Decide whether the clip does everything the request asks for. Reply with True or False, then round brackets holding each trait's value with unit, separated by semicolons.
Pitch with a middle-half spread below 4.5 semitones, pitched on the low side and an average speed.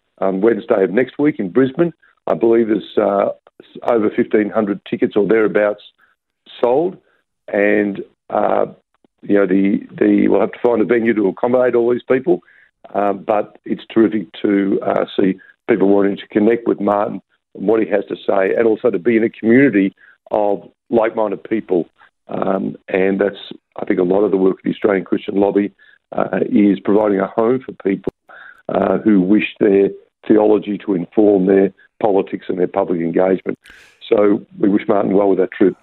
True (2.8 semitones; 105 Hz; 180 wpm)